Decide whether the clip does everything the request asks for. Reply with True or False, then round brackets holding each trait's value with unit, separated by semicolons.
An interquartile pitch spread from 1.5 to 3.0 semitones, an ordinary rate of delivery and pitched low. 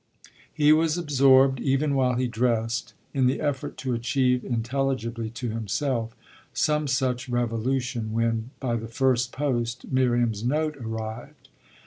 False (2.7 semitones; 130 wpm; 125 Hz)